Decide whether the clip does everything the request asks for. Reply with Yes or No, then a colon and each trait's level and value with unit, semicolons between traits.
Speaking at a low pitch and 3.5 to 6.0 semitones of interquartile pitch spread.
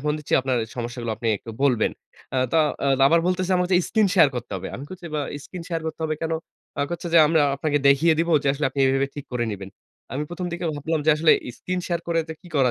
No: medium, 155 Hz; average, 4.3 semitones